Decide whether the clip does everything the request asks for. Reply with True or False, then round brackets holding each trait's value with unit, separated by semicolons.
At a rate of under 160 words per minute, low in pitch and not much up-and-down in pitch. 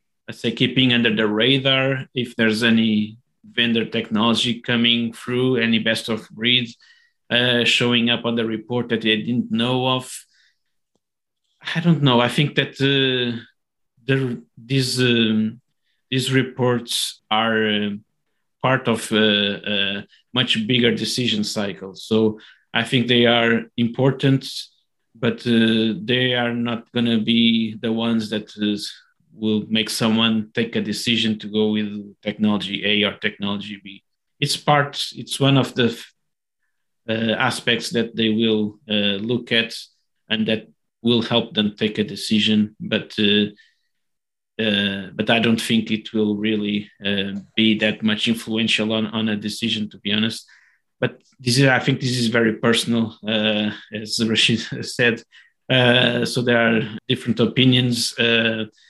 True (150 wpm; 115 Hz; 2.1 semitones)